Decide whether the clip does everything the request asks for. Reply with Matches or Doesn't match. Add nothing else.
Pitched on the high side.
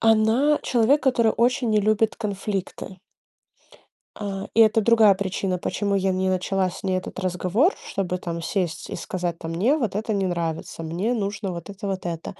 Matches